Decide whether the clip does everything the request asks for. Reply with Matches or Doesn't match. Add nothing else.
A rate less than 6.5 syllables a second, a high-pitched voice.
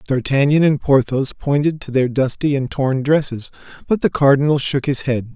Doesn't match